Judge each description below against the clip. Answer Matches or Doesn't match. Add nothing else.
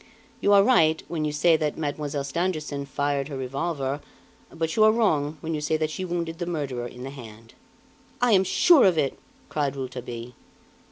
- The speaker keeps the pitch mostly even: Doesn't match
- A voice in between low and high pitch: Matches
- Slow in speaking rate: Doesn't match